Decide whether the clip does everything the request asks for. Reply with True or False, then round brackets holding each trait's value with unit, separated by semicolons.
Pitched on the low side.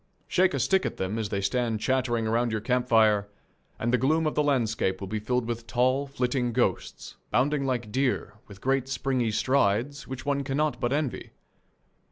True (125 Hz)